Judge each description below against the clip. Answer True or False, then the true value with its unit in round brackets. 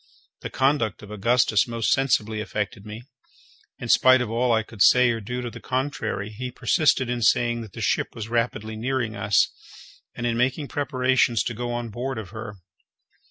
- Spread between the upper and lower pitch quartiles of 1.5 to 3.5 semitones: True (2.5 semitones)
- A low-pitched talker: True (120 Hz)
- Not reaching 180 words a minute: False (185 wpm)